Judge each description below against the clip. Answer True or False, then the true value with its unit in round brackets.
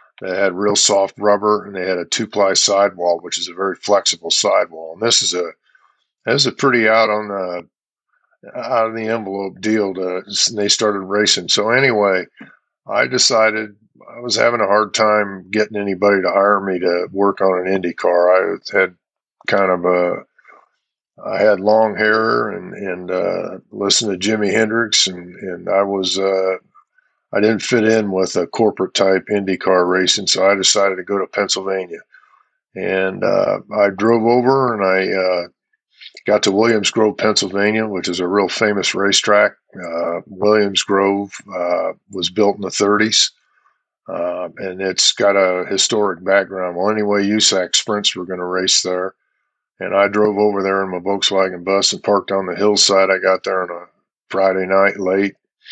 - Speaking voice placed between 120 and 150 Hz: False (100 Hz)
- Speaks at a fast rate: False (180 wpm)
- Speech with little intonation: True (2.1 semitones)